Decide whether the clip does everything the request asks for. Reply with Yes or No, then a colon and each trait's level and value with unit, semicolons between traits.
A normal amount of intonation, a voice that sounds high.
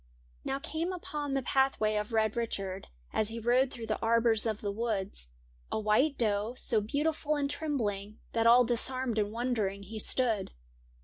Yes: average, 3.9 semitones; high, 230 Hz